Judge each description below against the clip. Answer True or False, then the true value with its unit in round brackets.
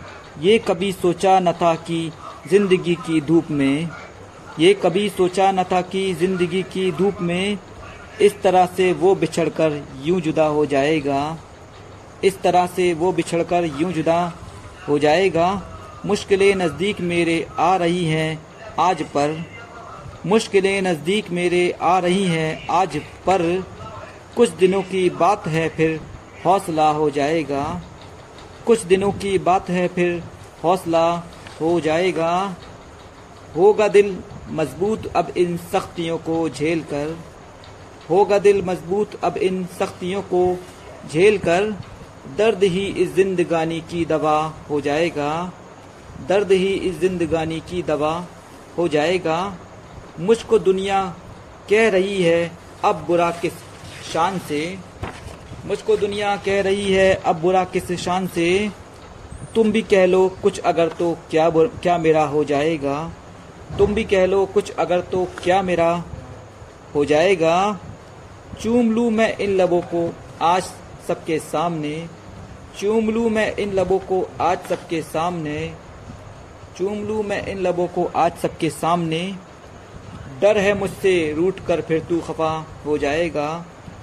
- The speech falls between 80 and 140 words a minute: True (135 wpm)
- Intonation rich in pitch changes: False (3.3 semitones)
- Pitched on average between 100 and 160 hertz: False (175 Hz)